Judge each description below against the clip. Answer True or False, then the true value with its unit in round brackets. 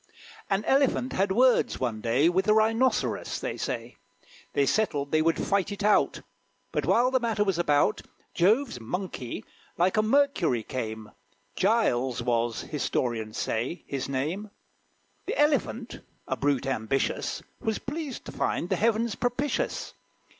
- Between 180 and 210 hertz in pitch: True (185 Hz)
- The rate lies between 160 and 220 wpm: False (140 wpm)